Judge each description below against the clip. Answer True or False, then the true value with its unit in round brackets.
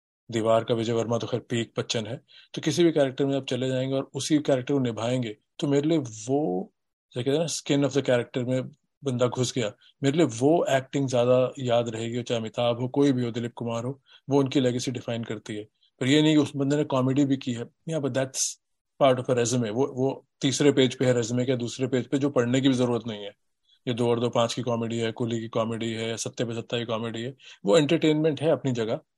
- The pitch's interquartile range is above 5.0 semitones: False (2.8 semitones)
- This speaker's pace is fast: True (245 wpm)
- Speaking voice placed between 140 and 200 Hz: False (125 Hz)